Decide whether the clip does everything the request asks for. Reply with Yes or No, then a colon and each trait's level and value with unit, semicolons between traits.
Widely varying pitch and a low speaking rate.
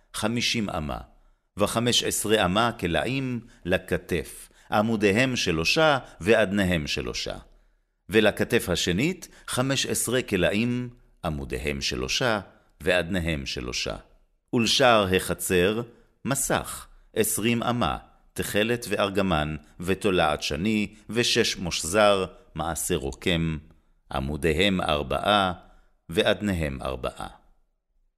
Yes: wide, 6.4 semitones; slow, 80 wpm